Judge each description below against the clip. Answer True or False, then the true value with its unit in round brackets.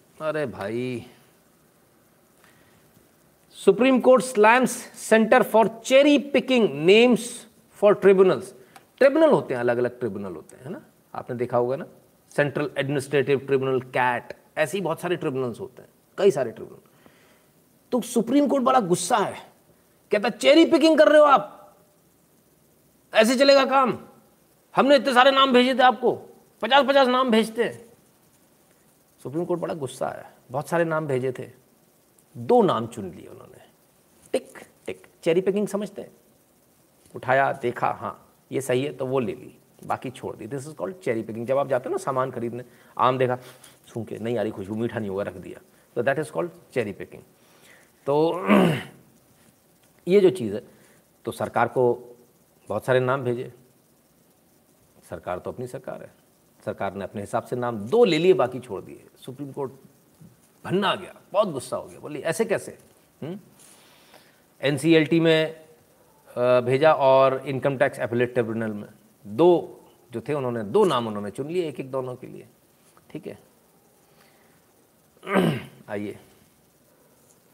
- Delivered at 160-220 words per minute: False (150 wpm)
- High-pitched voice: False (145 Hz)